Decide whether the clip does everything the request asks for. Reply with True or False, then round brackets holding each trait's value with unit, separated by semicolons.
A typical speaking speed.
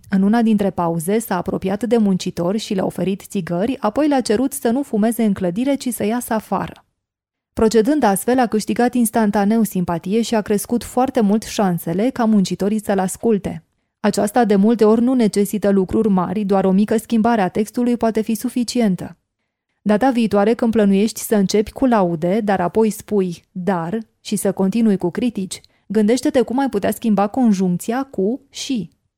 False (170 wpm)